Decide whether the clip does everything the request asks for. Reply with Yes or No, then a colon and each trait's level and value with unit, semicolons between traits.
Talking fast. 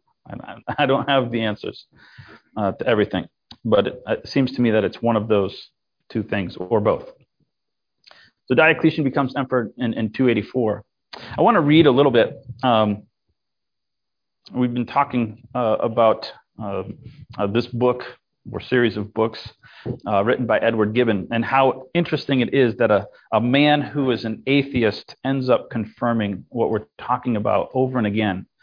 No: average, 165 wpm